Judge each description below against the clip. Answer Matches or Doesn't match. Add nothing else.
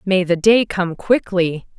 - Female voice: Matches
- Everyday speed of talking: Matches